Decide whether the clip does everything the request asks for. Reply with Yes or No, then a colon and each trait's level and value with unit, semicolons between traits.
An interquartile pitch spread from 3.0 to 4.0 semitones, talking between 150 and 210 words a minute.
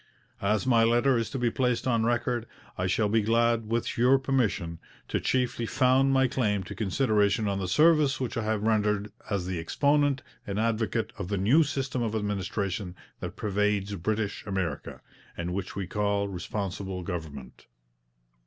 Yes: average, 3.7 semitones; average, 165 wpm